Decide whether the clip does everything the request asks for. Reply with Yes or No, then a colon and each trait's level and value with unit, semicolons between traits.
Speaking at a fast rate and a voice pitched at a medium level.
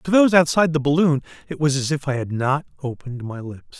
Yes: fast, 235 wpm; medium, 145 Hz